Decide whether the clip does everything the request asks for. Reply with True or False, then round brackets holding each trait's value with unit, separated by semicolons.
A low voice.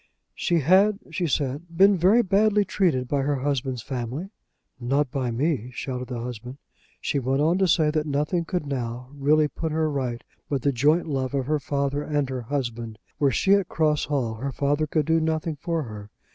False (145 Hz)